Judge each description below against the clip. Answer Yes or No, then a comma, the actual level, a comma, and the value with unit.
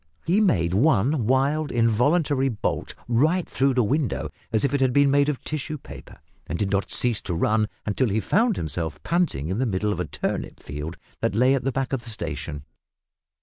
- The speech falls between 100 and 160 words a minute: No, average, 200 wpm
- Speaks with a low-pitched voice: Yes, low, 125 Hz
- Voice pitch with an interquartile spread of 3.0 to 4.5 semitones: No, wide, 5.6 semitones